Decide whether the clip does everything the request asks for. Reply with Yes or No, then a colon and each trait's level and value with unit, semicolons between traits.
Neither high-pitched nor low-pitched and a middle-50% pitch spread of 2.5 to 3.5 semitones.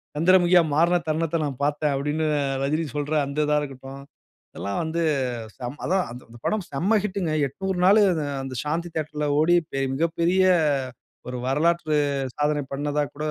Yes: medium, 150 Hz; average, 3.2 semitones